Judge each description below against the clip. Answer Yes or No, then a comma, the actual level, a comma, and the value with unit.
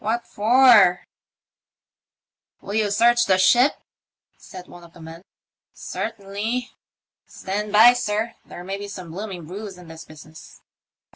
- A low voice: No, high, 200 Hz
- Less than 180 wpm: Yes, average, 160 wpm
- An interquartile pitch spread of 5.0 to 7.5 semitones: No, average, 3.7 semitones